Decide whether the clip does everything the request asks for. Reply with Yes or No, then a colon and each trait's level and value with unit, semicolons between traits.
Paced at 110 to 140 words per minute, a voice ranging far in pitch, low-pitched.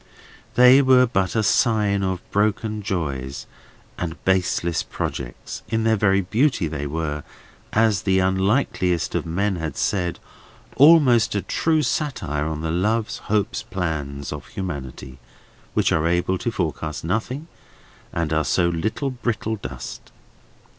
Yes: slow, 135 wpm; wide, 5.7 semitones; very low, 95 Hz